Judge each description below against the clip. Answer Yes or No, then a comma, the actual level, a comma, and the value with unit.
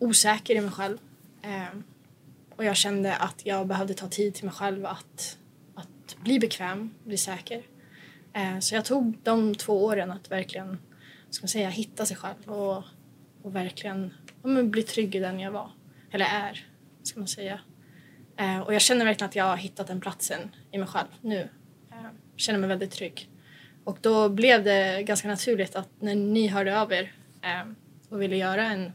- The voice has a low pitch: No, high, 195 Hz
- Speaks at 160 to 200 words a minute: Yes, average, 185 wpm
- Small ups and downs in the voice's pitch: Yes, narrow, 2.3 semitones